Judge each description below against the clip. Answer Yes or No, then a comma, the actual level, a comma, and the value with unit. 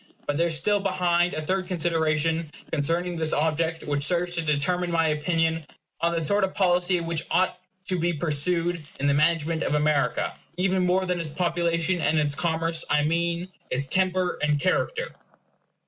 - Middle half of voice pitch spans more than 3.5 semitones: No, narrow, 2.5 semitones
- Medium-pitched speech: Yes, medium, 170 Hz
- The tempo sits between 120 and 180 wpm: Yes, average, 175 wpm